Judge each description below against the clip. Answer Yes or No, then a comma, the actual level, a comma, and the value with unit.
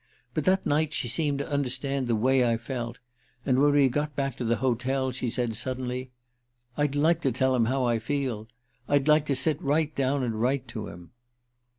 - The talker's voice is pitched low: Yes, low, 130 Hz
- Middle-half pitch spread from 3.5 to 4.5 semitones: No, average, 2.9 semitones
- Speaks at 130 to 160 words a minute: No, fast, 205 wpm